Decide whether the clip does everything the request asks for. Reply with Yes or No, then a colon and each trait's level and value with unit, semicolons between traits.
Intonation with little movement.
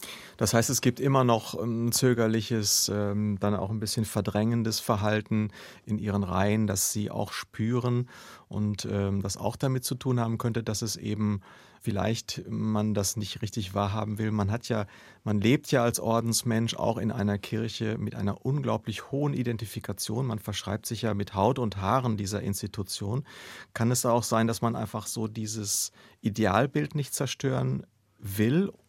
Yes: narrow, 2.1 semitones